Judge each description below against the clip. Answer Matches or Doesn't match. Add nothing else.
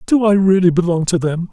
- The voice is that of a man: Matches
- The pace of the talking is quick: Matches